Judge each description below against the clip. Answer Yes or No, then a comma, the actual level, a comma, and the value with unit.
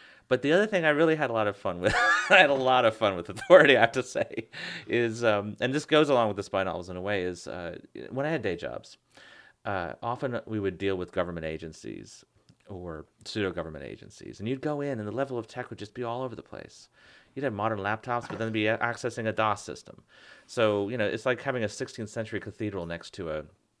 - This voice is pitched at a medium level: No, low, 110 Hz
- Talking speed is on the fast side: Yes, fast, 240 wpm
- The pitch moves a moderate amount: Yes, average, 3.9 semitones